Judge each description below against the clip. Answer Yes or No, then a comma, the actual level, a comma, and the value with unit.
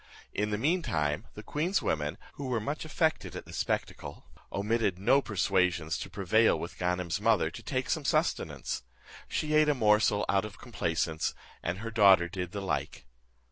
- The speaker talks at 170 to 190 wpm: Yes, average, 175 wpm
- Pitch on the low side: Yes, low, 105 Hz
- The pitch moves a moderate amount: Yes, average, 4.7 semitones